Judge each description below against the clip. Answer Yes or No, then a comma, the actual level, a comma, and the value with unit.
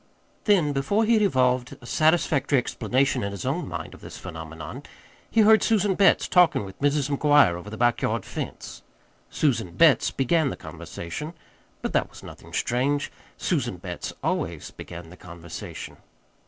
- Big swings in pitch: Yes, wide, 8.9 semitones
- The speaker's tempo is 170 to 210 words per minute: No, average, 160 wpm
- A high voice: No, low, 135 Hz